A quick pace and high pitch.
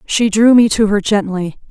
Yes: fast, 210 wpm; high, 210 Hz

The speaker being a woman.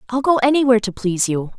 Yes: female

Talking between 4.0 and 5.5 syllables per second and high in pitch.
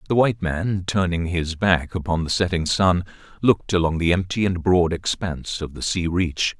No: 5.0 syllables/s; very low, 90 Hz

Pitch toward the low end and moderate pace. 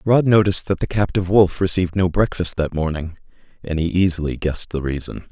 Yes: very low, 90 Hz; average, 190 wpm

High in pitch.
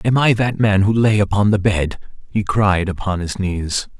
No: low, 100 Hz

